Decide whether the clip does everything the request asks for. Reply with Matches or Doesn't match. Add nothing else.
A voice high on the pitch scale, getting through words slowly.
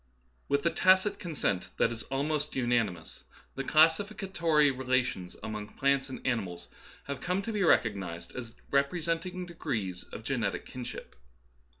Doesn't match